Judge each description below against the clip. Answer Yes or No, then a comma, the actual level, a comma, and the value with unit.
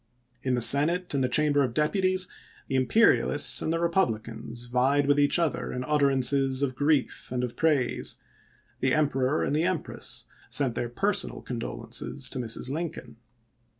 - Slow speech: No, average, 155 wpm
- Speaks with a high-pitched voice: No, medium, 140 Hz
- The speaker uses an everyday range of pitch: Yes, average, 3.5 semitones